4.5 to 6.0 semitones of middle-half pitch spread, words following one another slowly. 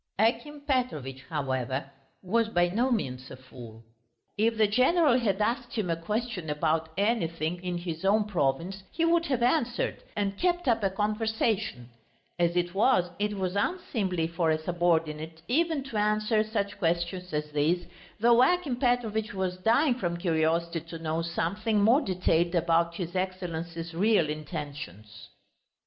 No: wide, 5.5 semitones; average, 150 wpm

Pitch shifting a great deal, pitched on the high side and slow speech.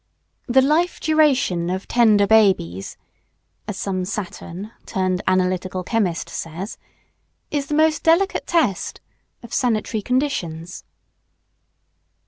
Yes: wide, 7.0 semitones; high, 210 Hz; slow, 105 wpm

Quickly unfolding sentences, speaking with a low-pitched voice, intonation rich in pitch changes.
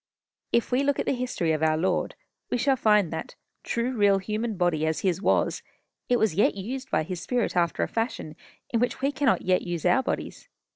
No: fast, 210 wpm; high, 210 Hz; wide, 6.0 semitones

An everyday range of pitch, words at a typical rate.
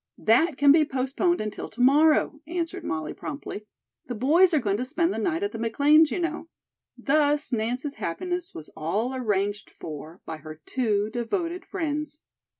No: wide, 7.0 semitones; average, 165 wpm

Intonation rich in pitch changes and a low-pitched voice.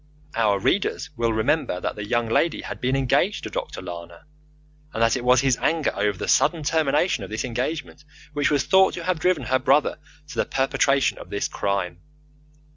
Yes: wide, 5.7 semitones; low, 130 Hz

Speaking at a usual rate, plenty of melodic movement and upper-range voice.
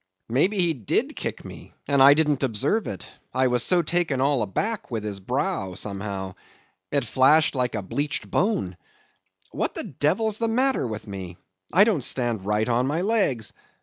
No: average, 175 wpm; wide, 8.4 semitones; low, 135 Hz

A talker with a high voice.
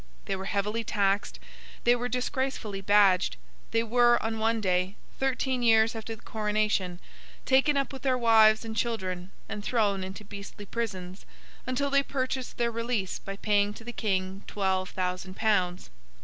Yes: high, 215 Hz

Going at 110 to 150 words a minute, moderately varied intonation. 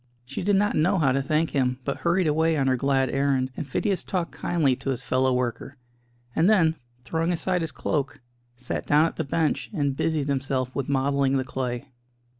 No: average, 200 wpm; average, 3.6 semitones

